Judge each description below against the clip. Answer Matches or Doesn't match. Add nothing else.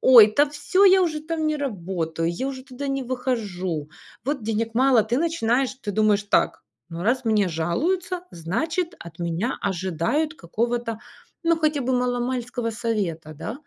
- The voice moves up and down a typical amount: Doesn't match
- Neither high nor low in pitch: Doesn't match